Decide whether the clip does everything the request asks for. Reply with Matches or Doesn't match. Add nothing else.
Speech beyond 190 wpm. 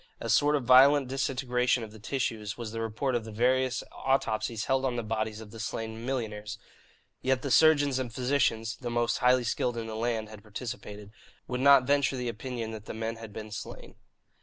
Matches